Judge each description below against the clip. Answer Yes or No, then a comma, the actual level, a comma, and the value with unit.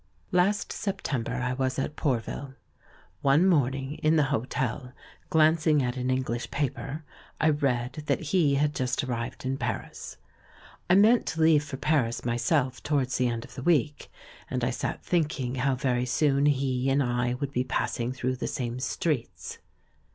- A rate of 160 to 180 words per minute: Yes, average, 165 wpm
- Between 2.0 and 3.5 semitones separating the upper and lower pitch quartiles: Yes, average, 3.1 semitones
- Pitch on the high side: No, low, 135 Hz